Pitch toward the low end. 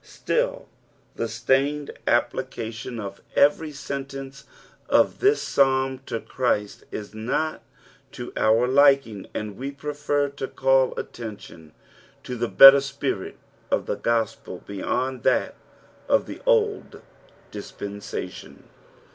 Yes: low, 130 Hz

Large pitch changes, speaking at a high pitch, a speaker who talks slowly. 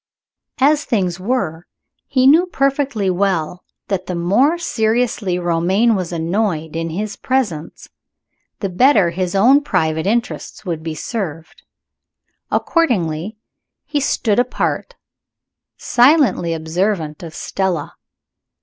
Yes: wide, 6.6 semitones; high, 195 Hz; slow, 110 wpm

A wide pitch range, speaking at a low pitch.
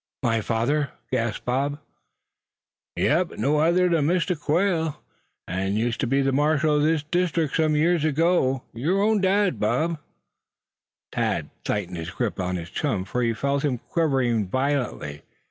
No: wide, 5.7 semitones; medium, 145 Hz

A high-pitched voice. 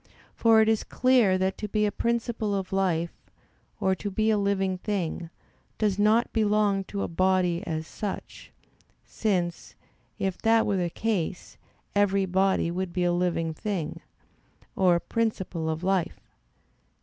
Yes: high, 195 Hz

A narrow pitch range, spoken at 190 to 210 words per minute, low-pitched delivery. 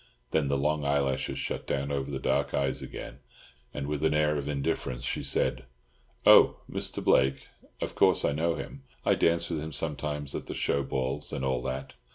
Yes: narrow, 2.0 semitones; average, 195 wpm; very low, 70 Hz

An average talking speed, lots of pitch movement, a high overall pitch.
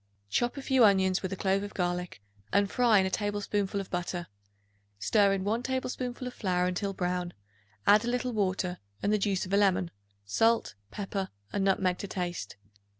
No: average, 185 wpm; narrow, 2.6 semitones; high, 195 Hz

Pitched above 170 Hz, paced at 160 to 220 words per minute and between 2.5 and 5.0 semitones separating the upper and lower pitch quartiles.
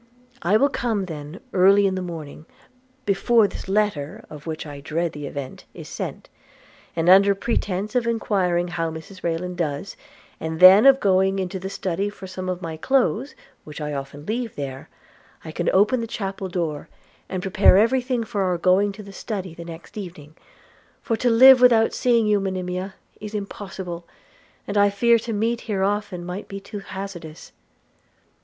Yes: high, 190 Hz; average, 175 wpm; average, 3.7 semitones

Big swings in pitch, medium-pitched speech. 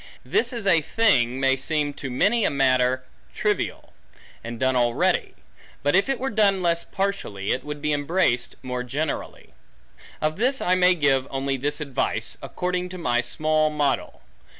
Yes: wide, 5.8 semitones; medium, 150 Hz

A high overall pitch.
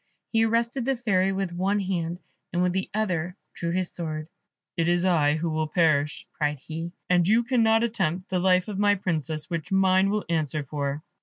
No: medium, 180 Hz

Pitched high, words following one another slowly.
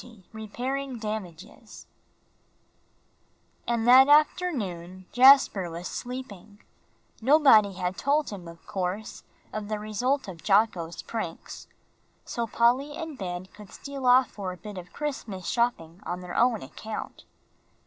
Yes: high, 215 Hz; slow, 130 wpm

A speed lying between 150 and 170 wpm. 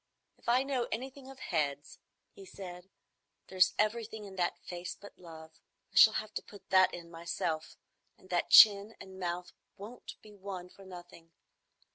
Yes: average, 165 wpm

